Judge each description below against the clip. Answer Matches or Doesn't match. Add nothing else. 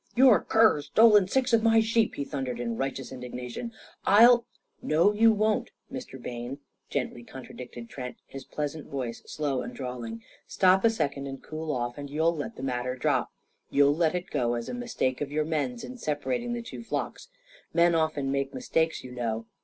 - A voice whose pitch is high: Doesn't match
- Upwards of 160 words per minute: Matches